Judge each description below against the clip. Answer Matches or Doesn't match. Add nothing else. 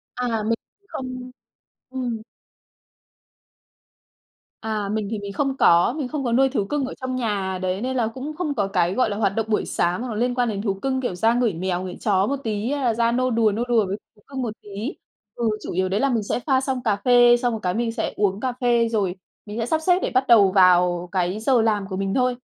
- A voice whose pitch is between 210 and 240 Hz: Matches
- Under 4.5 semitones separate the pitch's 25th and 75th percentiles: Matches